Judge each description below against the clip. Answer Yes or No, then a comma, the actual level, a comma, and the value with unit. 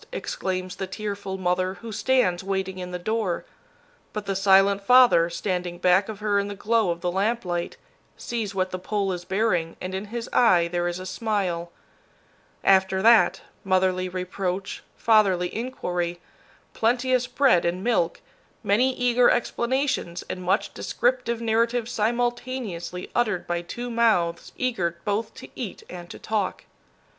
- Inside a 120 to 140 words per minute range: No, average, 150 wpm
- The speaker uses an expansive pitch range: No, average, 4.2 semitones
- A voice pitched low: No, high, 195 Hz